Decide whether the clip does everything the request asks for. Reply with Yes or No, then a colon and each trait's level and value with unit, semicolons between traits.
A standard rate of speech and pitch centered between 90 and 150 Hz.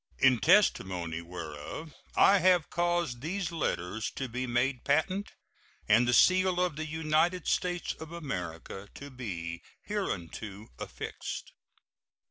No: slow, 120 wpm; low, 135 Hz